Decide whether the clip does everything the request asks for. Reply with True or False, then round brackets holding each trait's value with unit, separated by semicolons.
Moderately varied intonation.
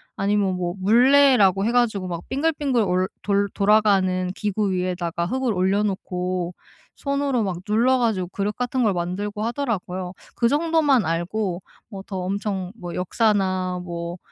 True (4.3 semitones)